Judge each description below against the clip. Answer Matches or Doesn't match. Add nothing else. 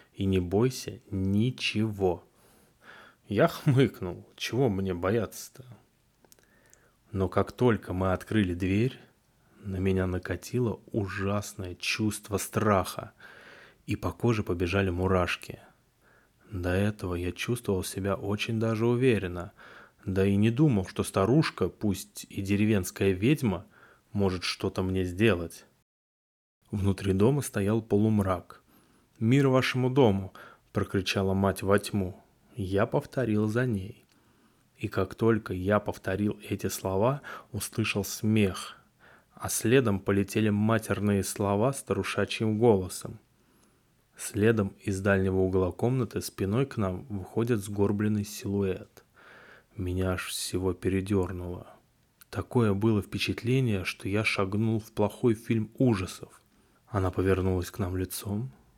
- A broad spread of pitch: Doesn't match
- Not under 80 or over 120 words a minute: Matches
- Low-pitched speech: Matches